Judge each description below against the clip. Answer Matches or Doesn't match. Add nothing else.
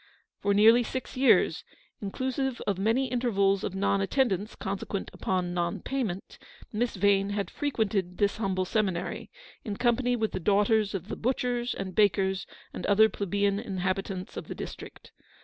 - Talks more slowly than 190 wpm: Matches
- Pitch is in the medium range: Doesn't match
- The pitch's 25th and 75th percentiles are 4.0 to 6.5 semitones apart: Doesn't match